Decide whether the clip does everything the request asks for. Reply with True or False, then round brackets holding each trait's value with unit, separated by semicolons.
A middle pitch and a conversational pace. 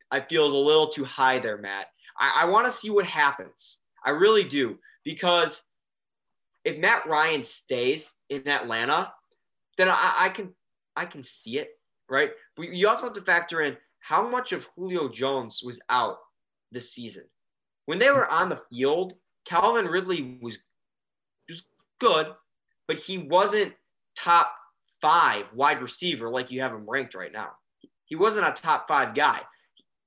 True (165 Hz; 160 wpm)